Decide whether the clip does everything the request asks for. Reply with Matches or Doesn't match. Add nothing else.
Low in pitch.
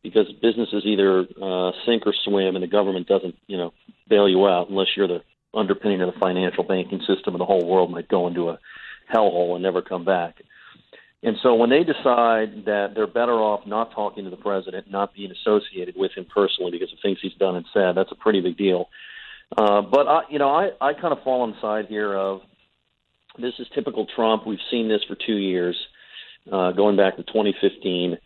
Matches